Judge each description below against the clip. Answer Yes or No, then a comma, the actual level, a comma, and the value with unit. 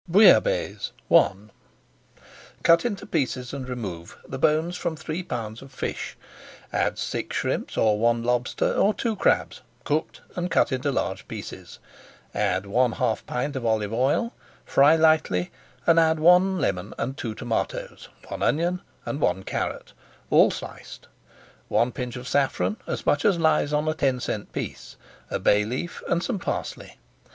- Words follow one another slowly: No, average, 155 wpm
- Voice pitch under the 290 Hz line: Yes, low, 135 Hz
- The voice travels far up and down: Yes, wide, 5.9 semitones